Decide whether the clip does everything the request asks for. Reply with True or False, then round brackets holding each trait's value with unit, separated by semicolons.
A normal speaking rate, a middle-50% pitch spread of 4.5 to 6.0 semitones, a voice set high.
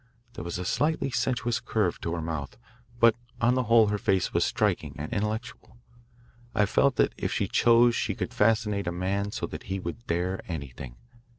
False (190 wpm; 5.2 semitones; 100 Hz)